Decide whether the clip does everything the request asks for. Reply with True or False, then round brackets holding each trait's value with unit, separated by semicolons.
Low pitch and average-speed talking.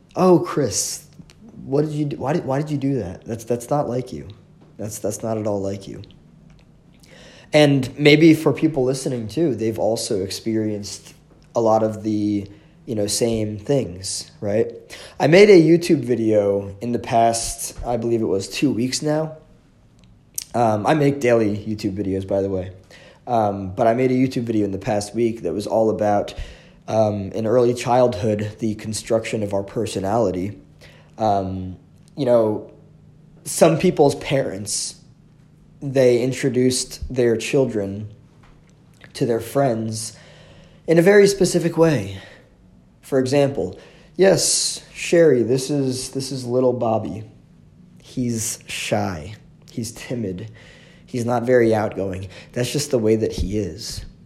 True (120 Hz; 150 wpm)